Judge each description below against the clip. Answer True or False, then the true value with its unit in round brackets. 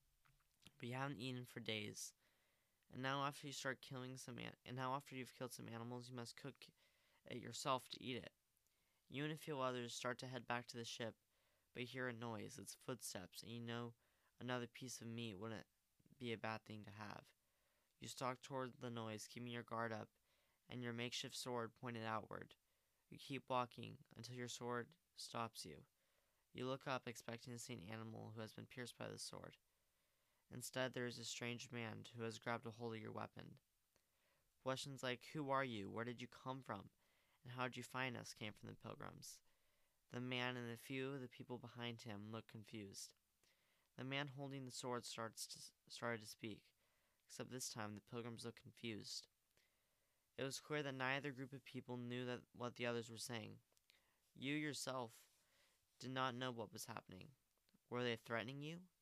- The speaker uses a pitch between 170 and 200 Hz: False (120 Hz)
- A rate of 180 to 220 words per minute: True (195 wpm)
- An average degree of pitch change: False (2.1 semitones)